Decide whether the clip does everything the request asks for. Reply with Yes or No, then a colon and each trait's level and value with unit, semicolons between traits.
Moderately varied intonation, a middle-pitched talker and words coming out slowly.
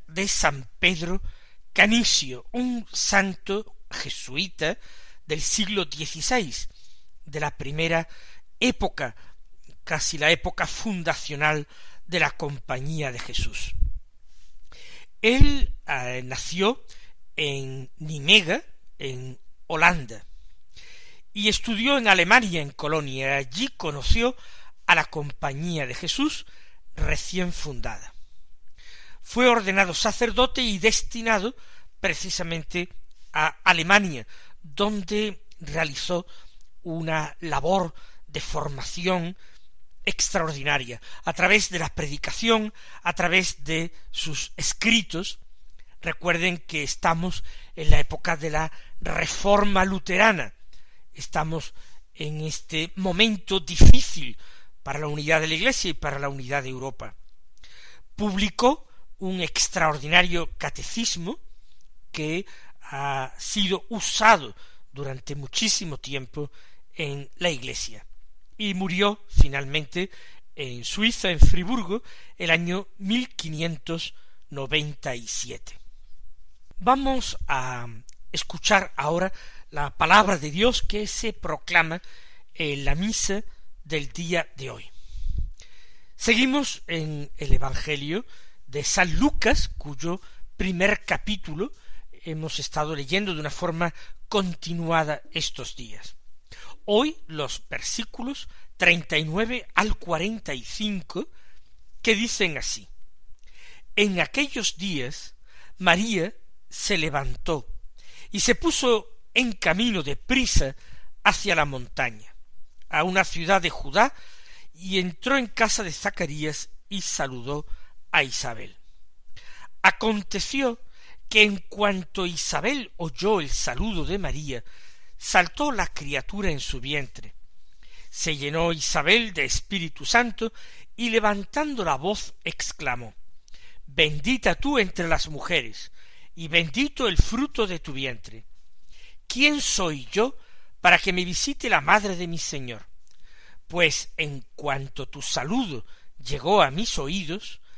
No: wide, 6.3 semitones; medium, 170 Hz; slow, 110 wpm